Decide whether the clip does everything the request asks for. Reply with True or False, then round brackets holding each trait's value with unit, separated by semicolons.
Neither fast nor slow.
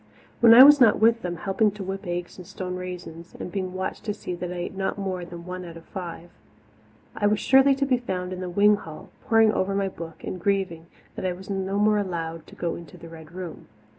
False (240 wpm)